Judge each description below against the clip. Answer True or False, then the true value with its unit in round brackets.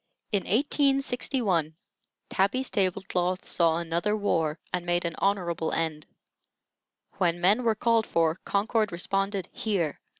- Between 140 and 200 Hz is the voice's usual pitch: True (190 Hz)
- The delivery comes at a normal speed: False (125 wpm)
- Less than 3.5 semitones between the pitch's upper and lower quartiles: False (4.0 semitones)